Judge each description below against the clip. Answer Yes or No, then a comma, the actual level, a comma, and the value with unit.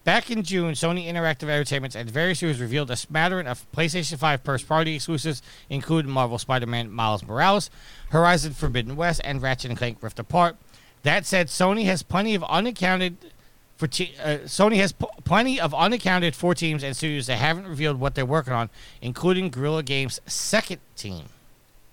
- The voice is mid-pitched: Yes, medium, 155 Hz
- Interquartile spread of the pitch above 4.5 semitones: Yes, average, 5.3 semitones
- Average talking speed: Yes, average, 170 wpm